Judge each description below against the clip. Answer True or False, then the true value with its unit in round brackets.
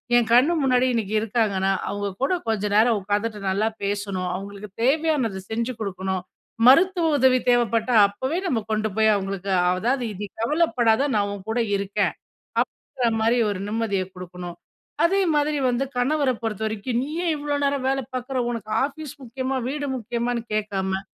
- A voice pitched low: False (225 Hz)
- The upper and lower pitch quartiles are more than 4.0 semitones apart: True (4.5 semitones)